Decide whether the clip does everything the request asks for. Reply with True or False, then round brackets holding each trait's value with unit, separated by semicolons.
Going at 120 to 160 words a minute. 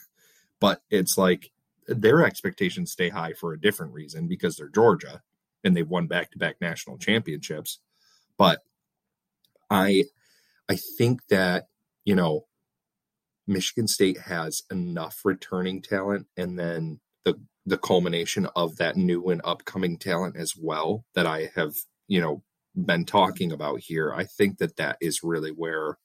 True (145 wpm)